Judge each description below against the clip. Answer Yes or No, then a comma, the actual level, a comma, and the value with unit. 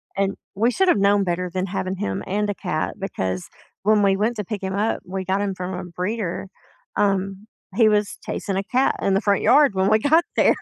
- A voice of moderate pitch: No, high, 195 Hz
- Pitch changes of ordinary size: No, narrow, 2.0 semitones